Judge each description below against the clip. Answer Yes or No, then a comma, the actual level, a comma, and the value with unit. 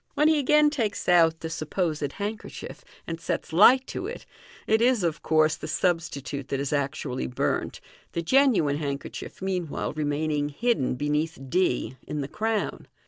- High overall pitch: No, medium, 160 Hz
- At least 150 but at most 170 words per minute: Yes, average, 155 wpm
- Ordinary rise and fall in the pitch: No, wide, 6.6 semitones